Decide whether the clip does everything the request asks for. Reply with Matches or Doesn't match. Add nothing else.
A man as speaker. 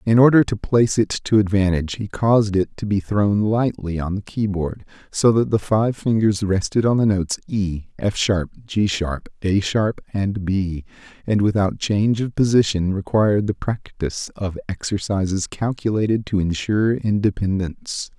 Matches